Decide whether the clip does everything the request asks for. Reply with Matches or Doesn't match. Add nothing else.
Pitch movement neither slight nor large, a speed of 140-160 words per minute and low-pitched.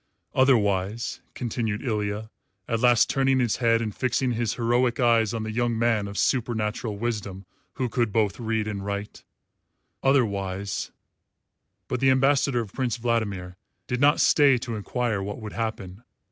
Matches